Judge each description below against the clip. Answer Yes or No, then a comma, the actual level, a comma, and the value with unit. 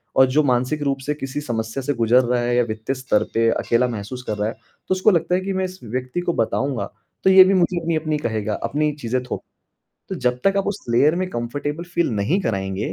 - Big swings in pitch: Yes, wide, 6.1 semitones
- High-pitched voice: No, low, 130 Hz